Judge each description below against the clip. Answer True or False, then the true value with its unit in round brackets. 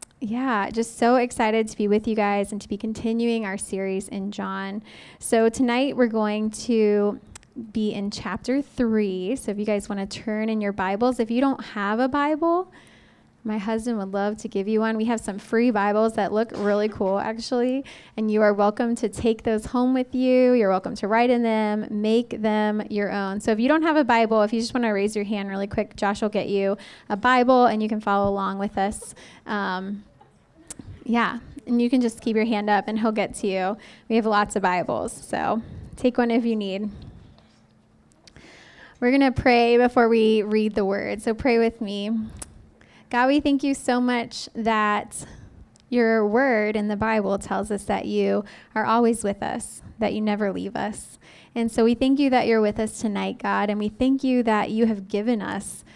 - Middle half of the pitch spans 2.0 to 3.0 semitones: True (2.4 semitones)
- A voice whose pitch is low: False (220 Hz)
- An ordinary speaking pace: False (210 wpm)